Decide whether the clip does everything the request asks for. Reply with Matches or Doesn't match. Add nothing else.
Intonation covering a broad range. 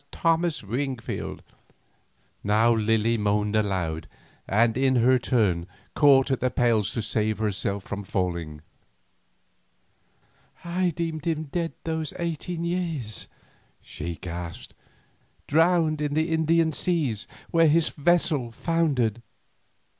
Matches